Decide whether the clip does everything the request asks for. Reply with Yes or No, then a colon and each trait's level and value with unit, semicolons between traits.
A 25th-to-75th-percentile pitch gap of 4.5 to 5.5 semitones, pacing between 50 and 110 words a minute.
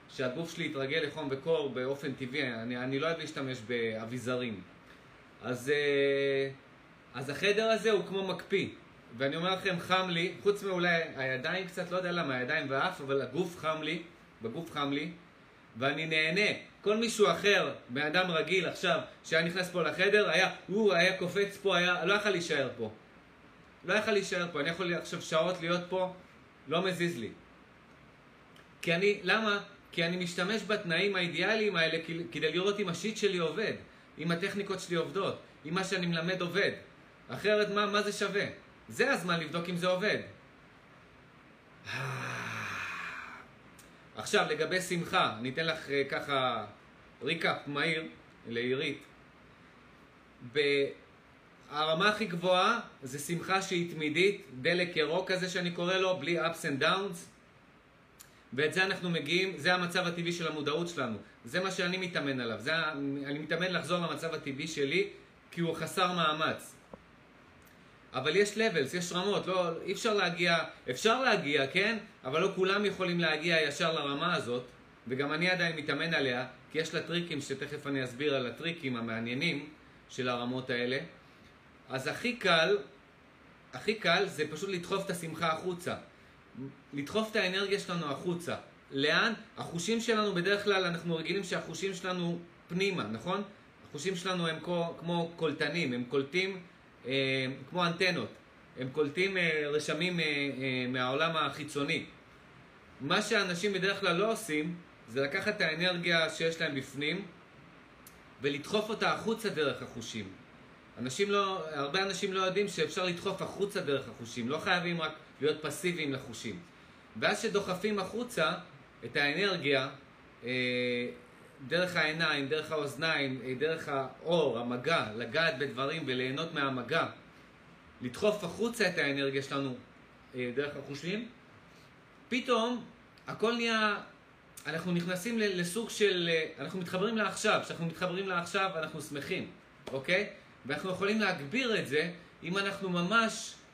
No: average, 5.0 semitones; average, 135 wpm